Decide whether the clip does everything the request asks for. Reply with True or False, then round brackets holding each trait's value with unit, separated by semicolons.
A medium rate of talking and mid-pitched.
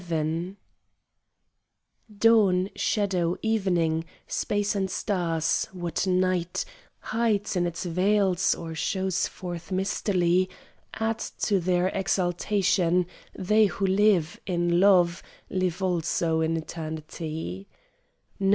False (95 wpm; 180 Hz)